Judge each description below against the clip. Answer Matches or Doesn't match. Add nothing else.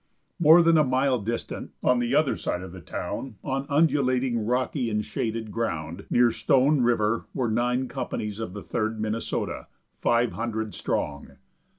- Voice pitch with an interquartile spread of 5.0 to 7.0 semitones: Doesn't match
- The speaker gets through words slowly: Doesn't match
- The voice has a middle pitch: Doesn't match